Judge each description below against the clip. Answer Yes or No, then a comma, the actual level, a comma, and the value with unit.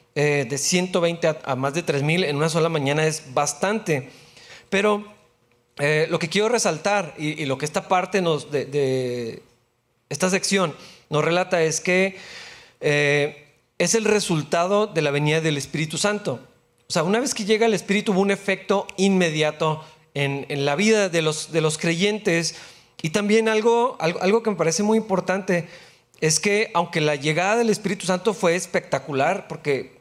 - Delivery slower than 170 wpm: No, average, 175 wpm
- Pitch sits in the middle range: Yes, medium, 170 Hz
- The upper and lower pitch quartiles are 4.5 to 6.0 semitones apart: Yes, average, 4.9 semitones